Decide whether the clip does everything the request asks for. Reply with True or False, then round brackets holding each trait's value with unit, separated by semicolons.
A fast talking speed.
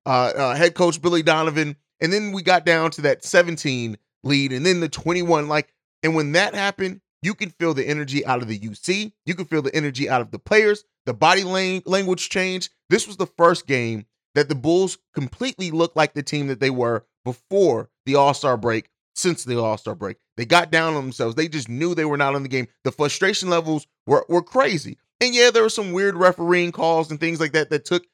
True (225 wpm)